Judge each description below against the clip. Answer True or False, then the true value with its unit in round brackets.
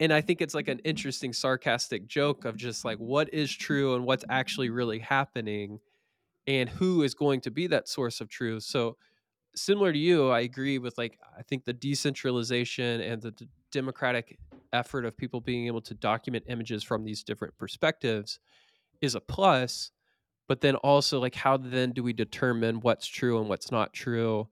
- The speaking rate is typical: True (185 wpm)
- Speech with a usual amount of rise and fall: True (3.0 semitones)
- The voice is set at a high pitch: False (125 Hz)